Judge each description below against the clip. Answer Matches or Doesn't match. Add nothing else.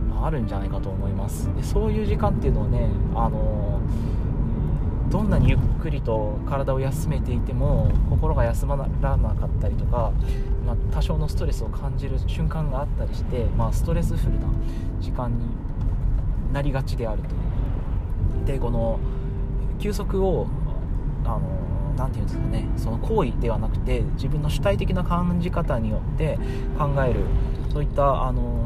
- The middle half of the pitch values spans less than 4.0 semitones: Doesn't match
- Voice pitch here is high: Doesn't match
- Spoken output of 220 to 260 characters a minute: Doesn't match